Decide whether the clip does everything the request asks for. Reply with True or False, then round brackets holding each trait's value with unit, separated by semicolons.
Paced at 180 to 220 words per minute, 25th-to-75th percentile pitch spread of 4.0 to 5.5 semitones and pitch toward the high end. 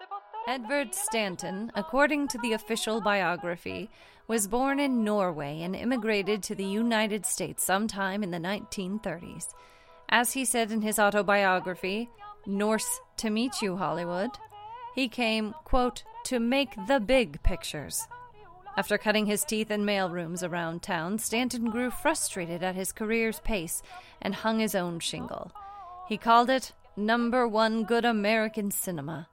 False (140 wpm; 4.3 semitones; 220 Hz)